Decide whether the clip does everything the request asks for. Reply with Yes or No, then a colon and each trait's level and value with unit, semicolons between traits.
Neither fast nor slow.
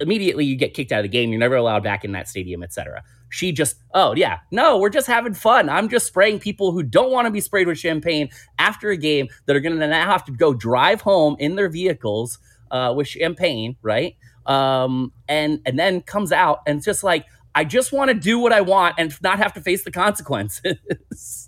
No: fast, 230 wpm